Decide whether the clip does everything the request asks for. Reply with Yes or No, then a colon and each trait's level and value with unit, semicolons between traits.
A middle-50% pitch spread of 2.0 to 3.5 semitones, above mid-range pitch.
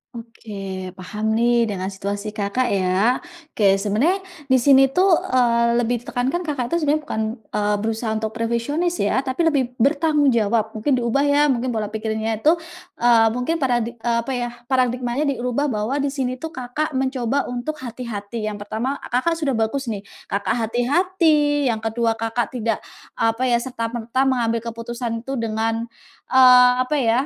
Yes: average, 2.8 semitones; high, 240 Hz